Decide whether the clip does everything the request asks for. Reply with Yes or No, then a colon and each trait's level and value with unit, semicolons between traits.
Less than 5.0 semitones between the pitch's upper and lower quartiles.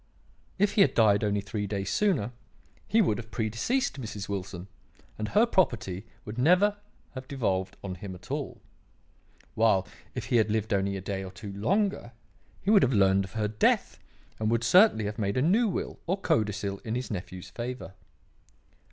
No: average, 5.3 semitones